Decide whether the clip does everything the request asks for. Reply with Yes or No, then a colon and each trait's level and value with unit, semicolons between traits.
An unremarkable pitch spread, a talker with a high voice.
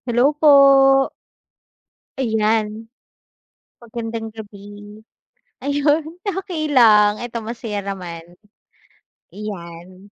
Yes: average, 3.8 semitones; high, 225 Hz